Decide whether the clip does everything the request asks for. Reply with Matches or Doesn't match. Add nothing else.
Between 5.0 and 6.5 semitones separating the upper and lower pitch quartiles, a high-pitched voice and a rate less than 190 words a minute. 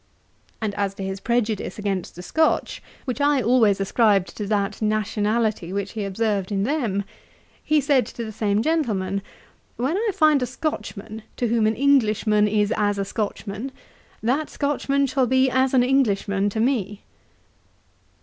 Doesn't match